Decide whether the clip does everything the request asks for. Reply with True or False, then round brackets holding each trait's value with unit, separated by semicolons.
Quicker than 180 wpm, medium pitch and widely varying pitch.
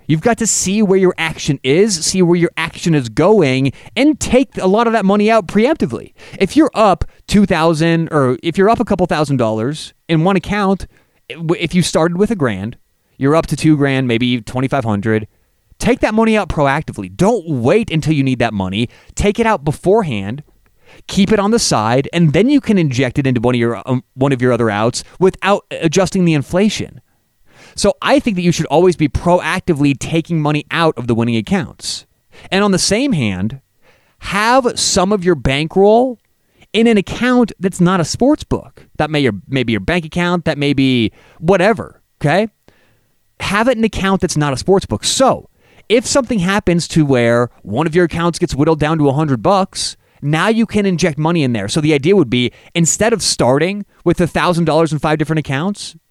True (200 wpm; 165 Hz; 6.4 semitones)